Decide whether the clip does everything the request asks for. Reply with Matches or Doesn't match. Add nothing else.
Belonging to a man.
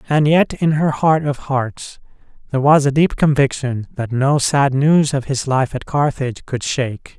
Matches